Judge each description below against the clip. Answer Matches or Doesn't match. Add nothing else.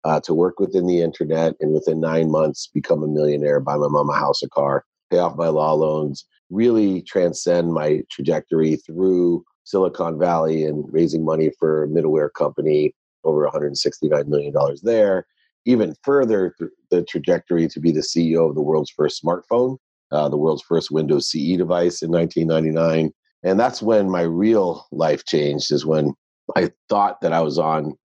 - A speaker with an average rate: Matches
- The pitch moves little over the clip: Matches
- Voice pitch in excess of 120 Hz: Doesn't match